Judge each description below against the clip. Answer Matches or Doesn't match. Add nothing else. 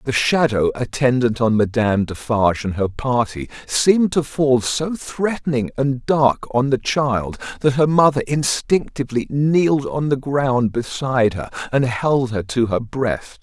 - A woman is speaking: Doesn't match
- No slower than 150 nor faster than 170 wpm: Matches